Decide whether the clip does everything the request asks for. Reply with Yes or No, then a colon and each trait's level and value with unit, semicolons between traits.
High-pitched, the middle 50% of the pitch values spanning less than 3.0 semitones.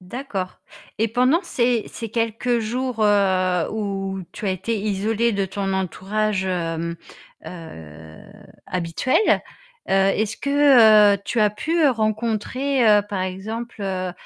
No: high, 210 Hz; average, 3.5 semitones